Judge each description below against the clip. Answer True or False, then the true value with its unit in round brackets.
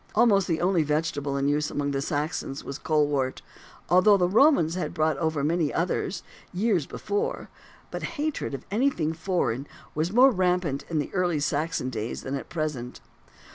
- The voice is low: False (160 Hz)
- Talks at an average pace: True (160 wpm)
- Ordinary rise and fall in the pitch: True (4.2 semitones)